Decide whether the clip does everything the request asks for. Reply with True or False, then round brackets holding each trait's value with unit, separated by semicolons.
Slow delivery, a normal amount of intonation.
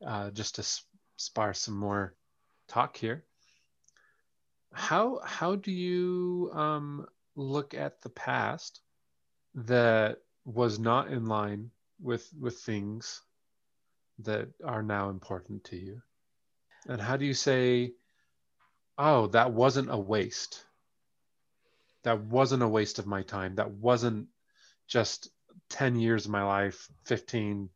True (125 wpm; 4.3 semitones)